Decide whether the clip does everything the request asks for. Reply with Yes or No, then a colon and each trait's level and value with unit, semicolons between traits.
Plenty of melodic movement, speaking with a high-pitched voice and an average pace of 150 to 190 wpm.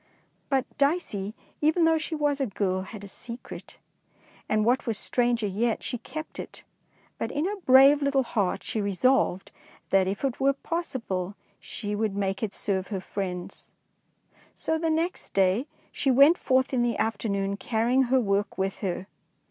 Yes: wide, 5.7 semitones; high, 235 Hz; average, 170 wpm